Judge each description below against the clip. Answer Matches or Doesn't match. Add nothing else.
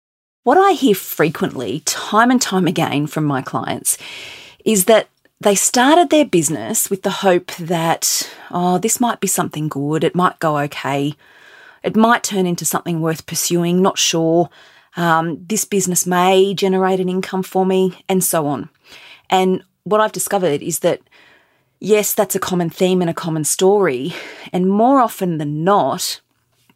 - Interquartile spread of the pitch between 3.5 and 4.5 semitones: Matches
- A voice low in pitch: Doesn't match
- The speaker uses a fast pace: Doesn't match